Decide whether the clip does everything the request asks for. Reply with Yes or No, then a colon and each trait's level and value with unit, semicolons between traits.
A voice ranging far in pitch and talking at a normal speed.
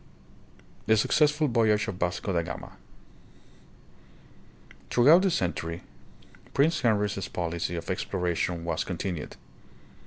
No: wide, 5.8 semitones; slow, 115 wpm